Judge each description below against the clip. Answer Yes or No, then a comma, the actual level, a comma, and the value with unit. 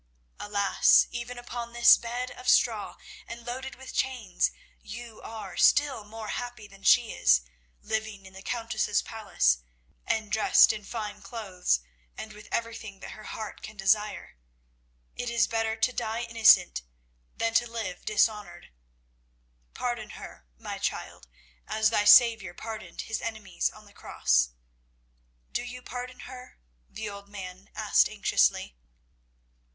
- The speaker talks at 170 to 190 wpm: No, average, 140 wpm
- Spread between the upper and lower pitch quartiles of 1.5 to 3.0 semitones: Yes, narrow, 2.6 semitones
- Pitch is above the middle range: Yes, high, 220 Hz